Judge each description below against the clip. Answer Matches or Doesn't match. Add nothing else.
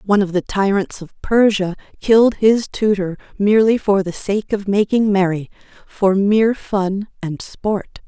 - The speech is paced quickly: Doesn't match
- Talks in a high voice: Matches